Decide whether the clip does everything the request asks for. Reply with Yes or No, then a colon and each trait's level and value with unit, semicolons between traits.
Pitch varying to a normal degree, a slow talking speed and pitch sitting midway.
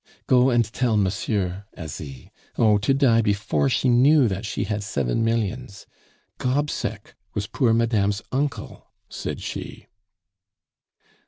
No: average, 3.8 semitones; slow, 120 wpm; low, 115 Hz